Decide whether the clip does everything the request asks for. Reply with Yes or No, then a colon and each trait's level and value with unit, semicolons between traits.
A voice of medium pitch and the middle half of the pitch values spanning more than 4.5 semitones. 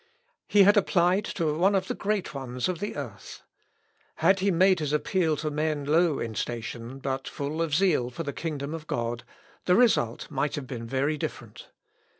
Yes: medium, 155 Hz; average, 5.2 semitones